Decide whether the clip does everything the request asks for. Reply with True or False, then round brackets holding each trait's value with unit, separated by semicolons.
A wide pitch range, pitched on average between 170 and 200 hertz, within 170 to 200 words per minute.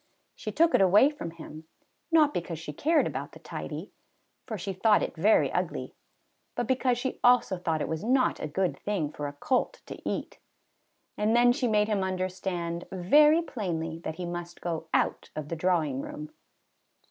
True (6.7 semitones; 185 Hz; 180 wpm)